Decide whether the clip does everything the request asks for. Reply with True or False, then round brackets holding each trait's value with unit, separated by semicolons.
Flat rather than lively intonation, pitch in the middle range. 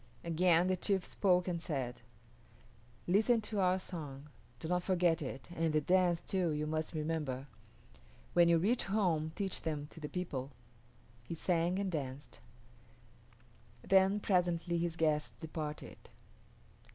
False (3.1 semitones; 170 Hz)